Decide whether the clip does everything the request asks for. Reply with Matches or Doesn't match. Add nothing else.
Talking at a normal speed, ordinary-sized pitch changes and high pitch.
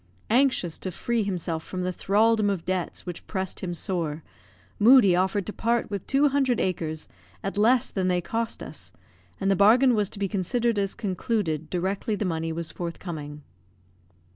Matches